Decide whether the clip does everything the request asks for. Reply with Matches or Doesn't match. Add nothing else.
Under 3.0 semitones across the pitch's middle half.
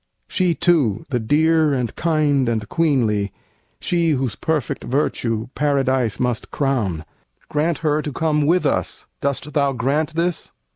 Doesn't match